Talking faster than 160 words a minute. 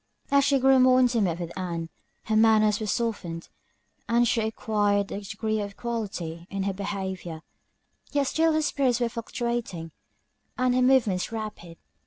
No: average, 155 wpm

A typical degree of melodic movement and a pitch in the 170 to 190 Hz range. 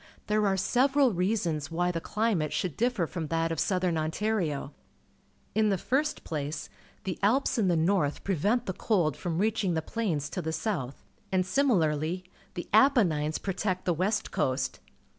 Yes: average, 5.0 semitones; medium, 185 Hz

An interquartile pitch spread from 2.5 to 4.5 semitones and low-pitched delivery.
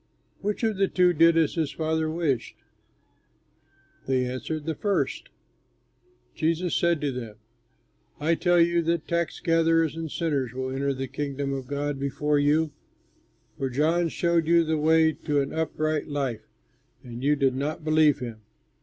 No: average, 3.0 semitones; medium, 155 Hz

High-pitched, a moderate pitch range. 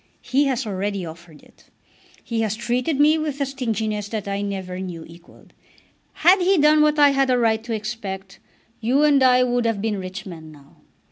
No: high, 225 Hz; wide, 5.8 semitones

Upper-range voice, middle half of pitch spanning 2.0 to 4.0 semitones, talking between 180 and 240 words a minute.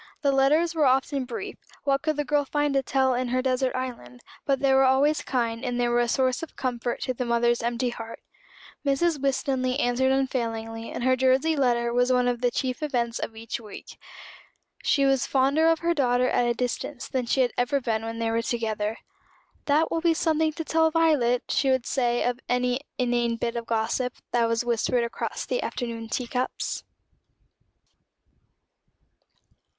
Yes: very high, 255 Hz; narrow, 2.5 semitones; average, 185 wpm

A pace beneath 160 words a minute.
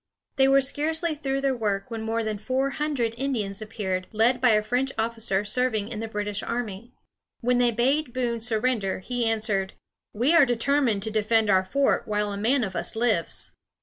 No: average, 185 wpm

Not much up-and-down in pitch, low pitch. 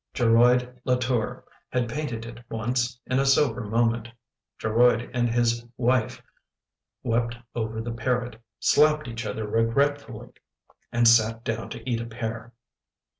Yes: narrow, 1.5 semitones; low, 120 Hz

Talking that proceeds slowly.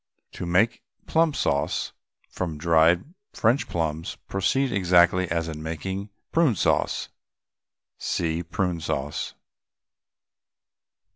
Yes: slow, 95 wpm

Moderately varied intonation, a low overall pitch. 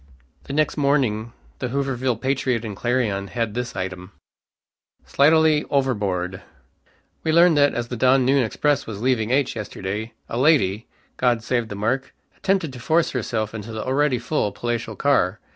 Yes: average, 4.3 semitones; low, 125 Hz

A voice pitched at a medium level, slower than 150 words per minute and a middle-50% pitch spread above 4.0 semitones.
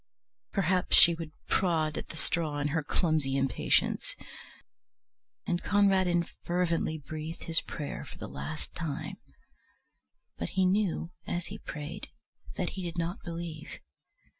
No: medium, 165 Hz; slow, 135 wpm; narrow, 2.4 semitones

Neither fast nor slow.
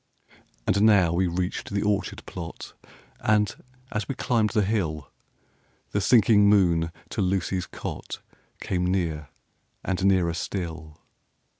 No: slow, 125 wpm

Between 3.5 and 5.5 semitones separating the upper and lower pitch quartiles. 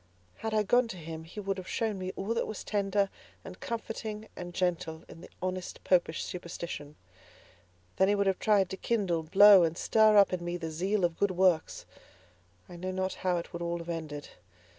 No: average, 3.0 semitones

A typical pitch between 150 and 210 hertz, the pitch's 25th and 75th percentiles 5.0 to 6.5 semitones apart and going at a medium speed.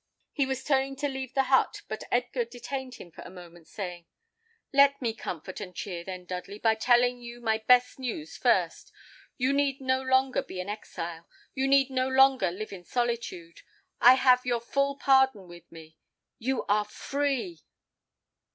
No: high, 245 Hz; wide, 5.5 semitones; average, 170 wpm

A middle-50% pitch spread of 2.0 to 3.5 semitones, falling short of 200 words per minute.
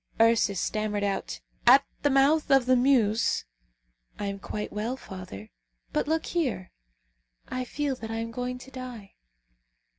No: average, 4.4 semitones; average, 155 wpm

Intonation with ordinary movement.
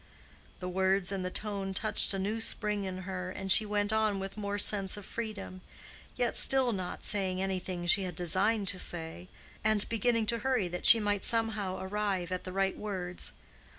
No: narrow, 2.3 semitones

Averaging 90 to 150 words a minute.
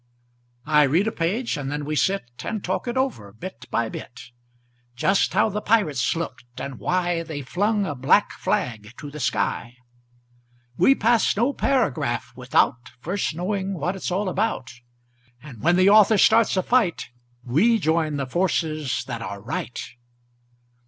No: average, 160 wpm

